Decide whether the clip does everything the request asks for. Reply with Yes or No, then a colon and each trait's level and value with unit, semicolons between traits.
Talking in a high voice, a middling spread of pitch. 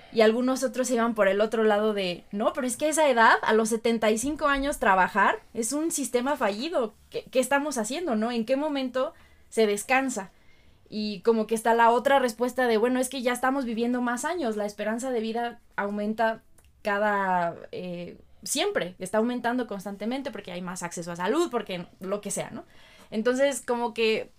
Yes: high, 230 Hz; average, 3.7 semitones